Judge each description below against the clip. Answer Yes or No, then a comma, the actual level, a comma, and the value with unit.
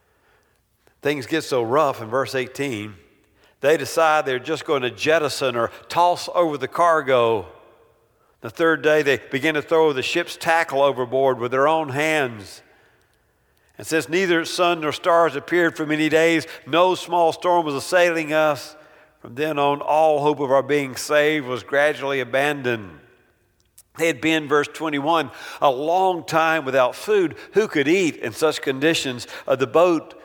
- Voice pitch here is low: No, medium, 155 Hz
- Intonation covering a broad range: No, average, 3.4 semitones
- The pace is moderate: Yes, average, 160 wpm